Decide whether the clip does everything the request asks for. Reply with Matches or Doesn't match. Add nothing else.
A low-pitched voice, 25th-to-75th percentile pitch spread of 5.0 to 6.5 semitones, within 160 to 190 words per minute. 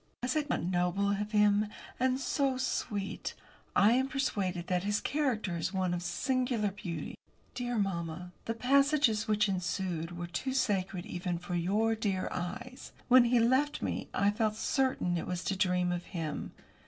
Doesn't match